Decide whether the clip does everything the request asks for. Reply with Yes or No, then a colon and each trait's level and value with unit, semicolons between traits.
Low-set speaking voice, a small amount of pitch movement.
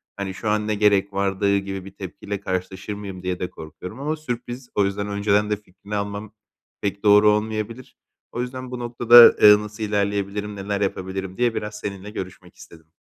Yes: low, 100 Hz; narrow, 1.6 semitones